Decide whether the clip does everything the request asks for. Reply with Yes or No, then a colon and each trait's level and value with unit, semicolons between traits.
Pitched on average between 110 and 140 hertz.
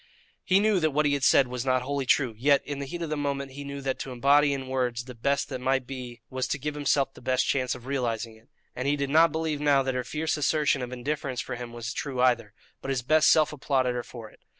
Yes: low, 135 Hz